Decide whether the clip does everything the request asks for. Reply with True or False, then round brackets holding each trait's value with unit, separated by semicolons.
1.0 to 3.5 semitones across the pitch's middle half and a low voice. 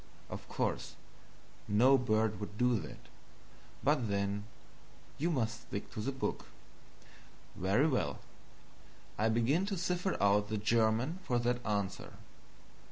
False (4.5 semitones; 115 Hz)